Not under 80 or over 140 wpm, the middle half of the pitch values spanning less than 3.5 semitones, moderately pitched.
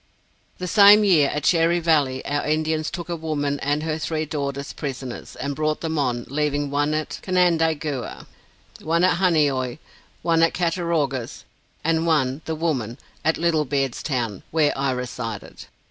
No: average, 155 wpm; average, 2.9 semitones; medium, 155 Hz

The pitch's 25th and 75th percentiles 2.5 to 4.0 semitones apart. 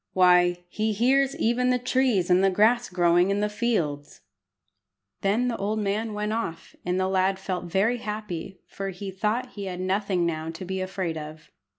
Yes: average, 3.4 semitones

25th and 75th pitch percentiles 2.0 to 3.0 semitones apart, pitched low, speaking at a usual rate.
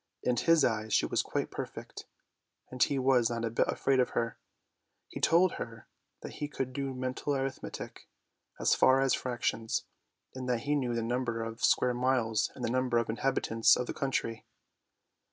Yes: narrow, 2.4 semitones; low, 125 Hz; average, 180 wpm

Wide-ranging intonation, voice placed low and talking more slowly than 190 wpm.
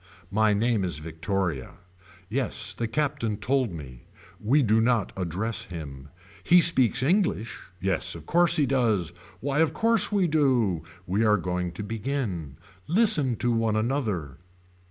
Yes: wide, 7.2 semitones; low, 110 Hz; average, 145 wpm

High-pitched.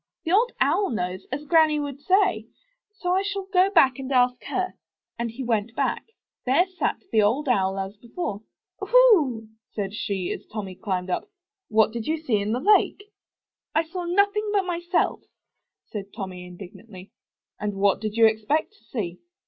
Yes: very high, 255 Hz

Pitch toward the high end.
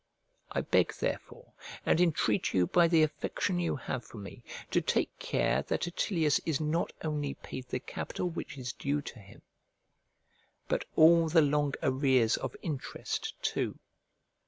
No: medium, 150 Hz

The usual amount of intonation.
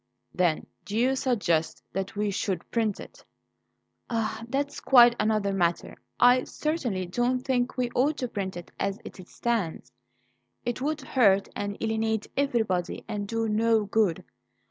Yes: average, 3.8 semitones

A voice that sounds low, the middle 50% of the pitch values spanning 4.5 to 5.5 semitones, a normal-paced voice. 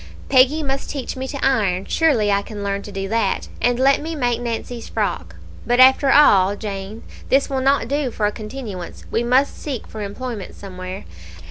No: high, 240 Hz; average, 4.9 semitones; average, 190 wpm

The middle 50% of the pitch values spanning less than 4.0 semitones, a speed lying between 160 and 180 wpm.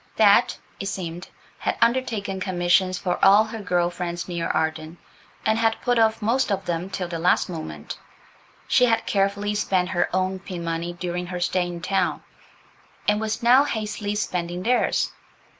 Yes: average, 3.4 semitones; average, 165 wpm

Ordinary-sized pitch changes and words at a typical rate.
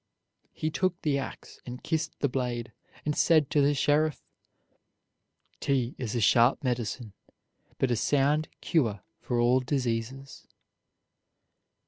No: average, 3.5 semitones; slow, 125 wpm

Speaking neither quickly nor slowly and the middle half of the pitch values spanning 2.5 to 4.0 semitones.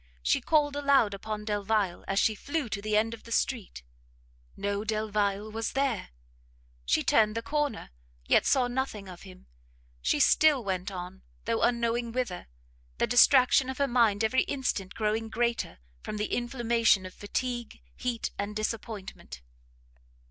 Yes: average, 150 wpm; average, 3.3 semitones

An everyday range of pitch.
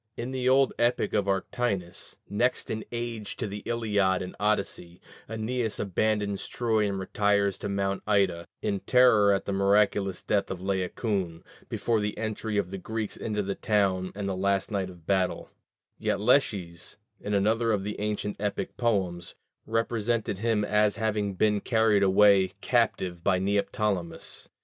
No: narrow, 2.2 semitones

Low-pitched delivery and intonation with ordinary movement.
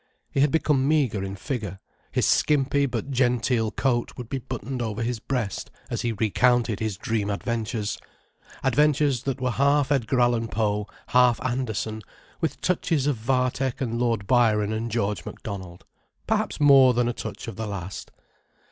Yes: low, 120 Hz; average, 3.4 semitones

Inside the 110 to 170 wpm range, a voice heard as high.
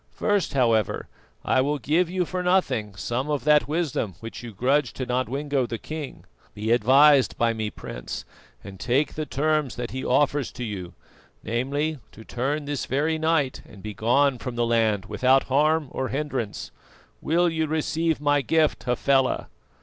No: average, 165 wpm; low, 135 Hz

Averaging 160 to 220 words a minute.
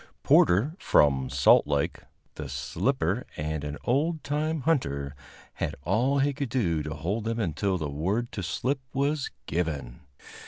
No: average, 150 wpm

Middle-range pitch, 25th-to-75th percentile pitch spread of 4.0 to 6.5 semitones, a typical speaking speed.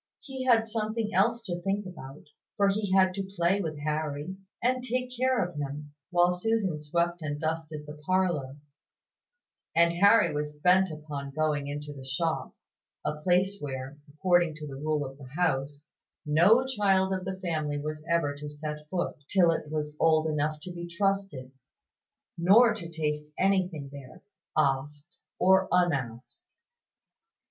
Yes: medium, 165 Hz; average, 4.3 semitones; average, 155 wpm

